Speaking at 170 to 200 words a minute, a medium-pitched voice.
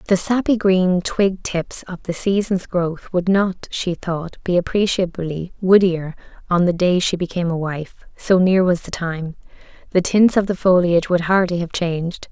Yes: average, 180 wpm; medium, 180 Hz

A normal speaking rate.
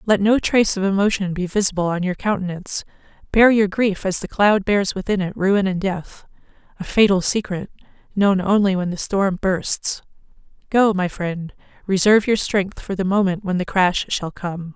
Yes: average, 180 wpm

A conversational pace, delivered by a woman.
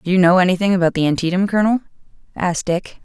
Yes: average, 195 wpm; female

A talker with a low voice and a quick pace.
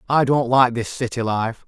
Yes: low, 120 Hz; fast, 215 wpm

